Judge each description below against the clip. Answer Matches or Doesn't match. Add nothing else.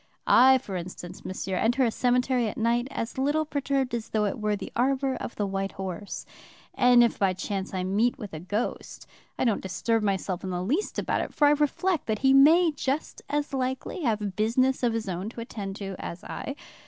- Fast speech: Matches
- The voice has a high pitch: Matches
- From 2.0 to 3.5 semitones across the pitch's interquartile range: Doesn't match